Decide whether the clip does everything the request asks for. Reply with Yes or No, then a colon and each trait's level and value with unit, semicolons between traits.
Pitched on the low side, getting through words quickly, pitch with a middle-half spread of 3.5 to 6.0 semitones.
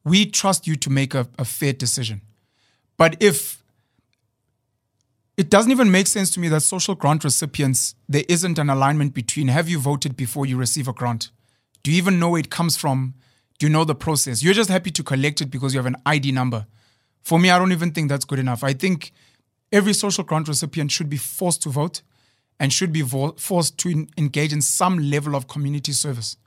No: medium, 145 Hz; fast, 210 wpm; average, 4.5 semitones